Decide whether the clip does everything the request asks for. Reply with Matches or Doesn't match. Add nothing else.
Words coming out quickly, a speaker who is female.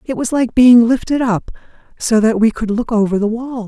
Matches